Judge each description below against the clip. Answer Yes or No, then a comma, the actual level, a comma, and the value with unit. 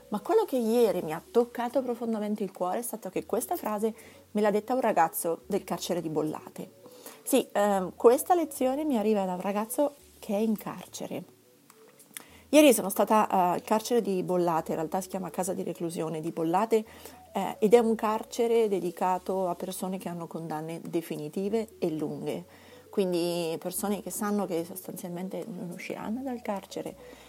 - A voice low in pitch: No, high, 200 Hz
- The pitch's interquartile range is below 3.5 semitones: No, average, 4.2 semitones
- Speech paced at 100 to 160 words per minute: No, fast, 170 wpm